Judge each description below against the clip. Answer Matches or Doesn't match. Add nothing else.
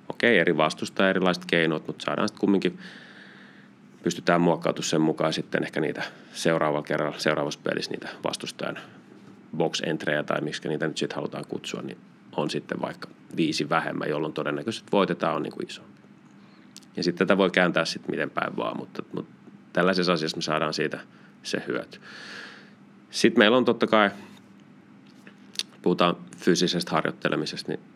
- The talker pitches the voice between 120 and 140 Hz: Doesn't match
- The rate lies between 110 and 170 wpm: Matches